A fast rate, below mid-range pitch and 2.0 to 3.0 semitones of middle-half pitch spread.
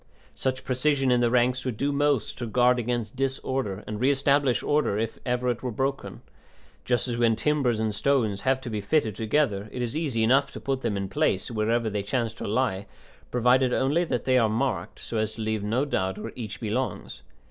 No: fast, 210 wpm; low, 125 Hz; average, 3.4 semitones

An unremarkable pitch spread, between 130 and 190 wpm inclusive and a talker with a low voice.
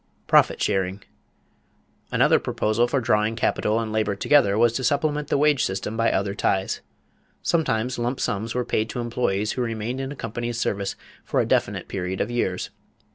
Yes: average, 3.2 semitones; average, 175 wpm; low, 115 Hz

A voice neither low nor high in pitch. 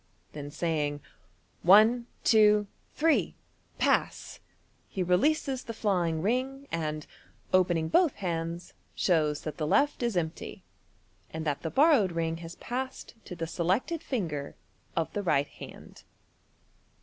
Yes: medium, 175 Hz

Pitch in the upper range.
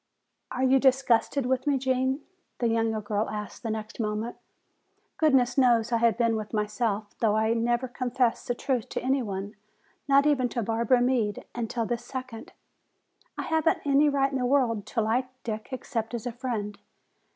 Yes: high, 240 Hz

